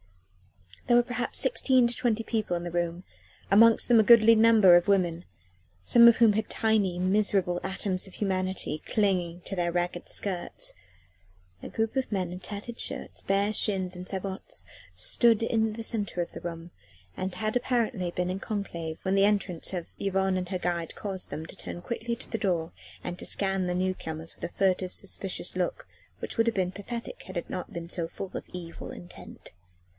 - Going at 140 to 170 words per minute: No, average, 190 wpm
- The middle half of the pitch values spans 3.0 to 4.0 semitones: Yes, average, 3.7 semitones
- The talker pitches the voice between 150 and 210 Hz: Yes, high, 190 Hz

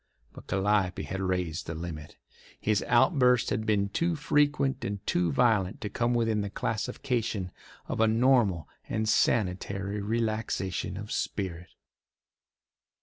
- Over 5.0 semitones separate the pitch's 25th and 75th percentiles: No, average, 3.9 semitones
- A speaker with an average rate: No, slow, 130 wpm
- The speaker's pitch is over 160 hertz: No, low, 105 Hz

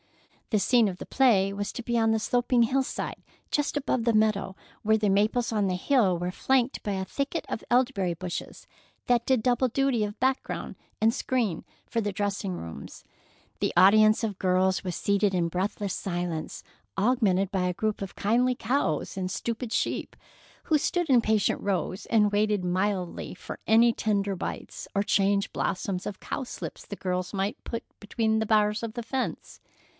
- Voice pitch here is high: Yes, high, 210 Hz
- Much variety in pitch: No, average, 3.8 semitones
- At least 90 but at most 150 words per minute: No, average, 175 wpm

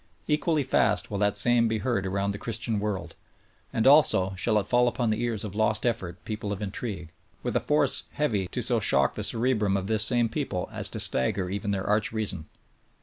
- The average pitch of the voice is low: Yes, low, 105 Hz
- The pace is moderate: No, fast, 210 wpm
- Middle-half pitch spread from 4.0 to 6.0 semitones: No, average, 3.4 semitones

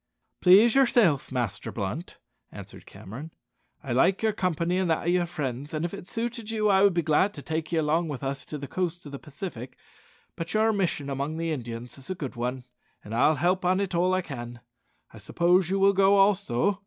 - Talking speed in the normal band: No, fast, 215 wpm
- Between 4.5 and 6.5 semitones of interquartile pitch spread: Yes, wide, 5.6 semitones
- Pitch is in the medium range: Yes, medium, 165 Hz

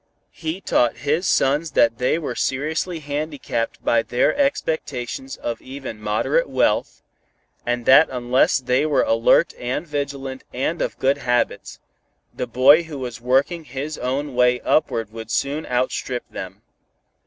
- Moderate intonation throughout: Yes, average, 3.5 semitones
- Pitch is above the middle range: No, low, 135 Hz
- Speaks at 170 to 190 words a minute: No, average, 145 wpm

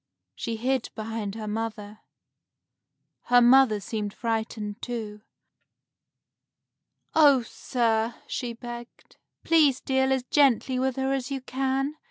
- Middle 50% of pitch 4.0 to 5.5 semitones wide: No, average, 3.1 semitones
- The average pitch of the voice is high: Yes, high, 240 Hz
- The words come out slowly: Yes, slow, 115 wpm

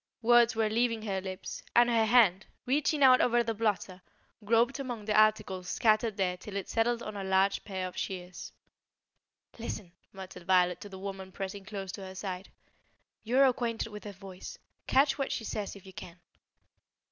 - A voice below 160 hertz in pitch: No, high, 210 Hz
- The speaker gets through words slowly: No, average, 180 wpm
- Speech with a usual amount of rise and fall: Yes, average, 3.5 semitones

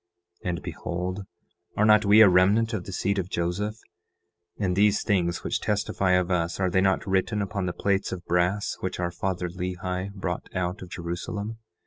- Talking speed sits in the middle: Yes, average, 180 wpm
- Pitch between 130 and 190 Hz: No, very low, 95 Hz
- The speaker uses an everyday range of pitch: No, narrow, 2.2 semitones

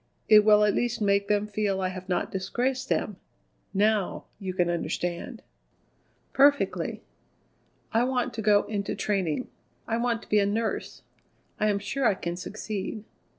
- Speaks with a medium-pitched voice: No, high, 210 Hz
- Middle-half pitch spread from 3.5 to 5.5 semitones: No, average, 2.7 semitones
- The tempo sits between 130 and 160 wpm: Yes, average, 155 wpm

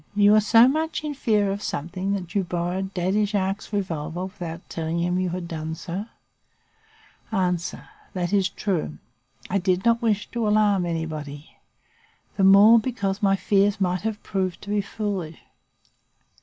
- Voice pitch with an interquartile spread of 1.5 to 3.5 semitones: Yes, average, 2.9 semitones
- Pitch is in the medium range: No, high, 195 Hz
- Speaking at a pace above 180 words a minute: No, average, 160 wpm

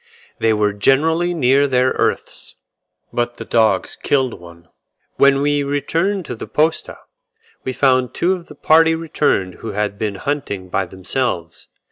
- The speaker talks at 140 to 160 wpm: Yes, average, 150 wpm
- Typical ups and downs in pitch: No, wide, 6.2 semitones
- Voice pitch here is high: No, low, 130 Hz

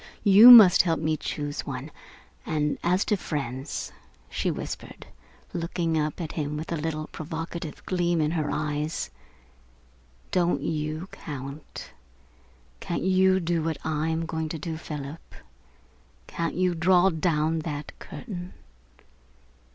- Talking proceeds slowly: Yes, slow, 130 wpm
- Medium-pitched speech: Yes, medium, 160 Hz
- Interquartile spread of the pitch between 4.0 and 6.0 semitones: No, narrow, 2.4 semitones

